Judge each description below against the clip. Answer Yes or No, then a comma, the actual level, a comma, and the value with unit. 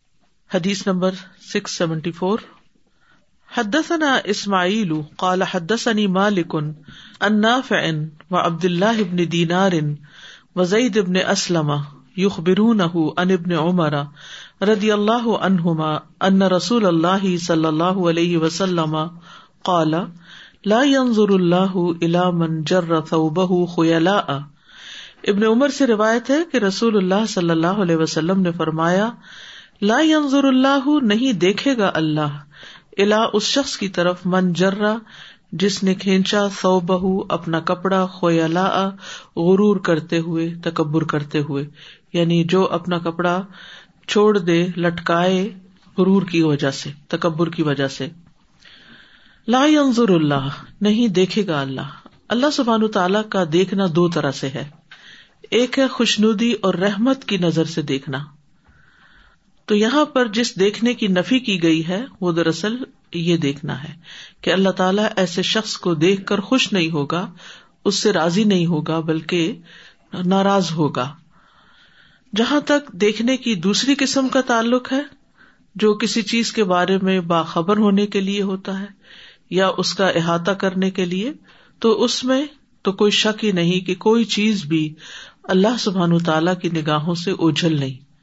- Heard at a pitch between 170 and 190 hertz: Yes, medium, 185 Hz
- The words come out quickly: No, average, 130 wpm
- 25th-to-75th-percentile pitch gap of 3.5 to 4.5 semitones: Yes, average, 4.0 semitones